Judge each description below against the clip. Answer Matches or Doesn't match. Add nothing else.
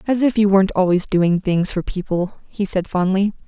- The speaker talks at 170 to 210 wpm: Matches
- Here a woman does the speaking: Matches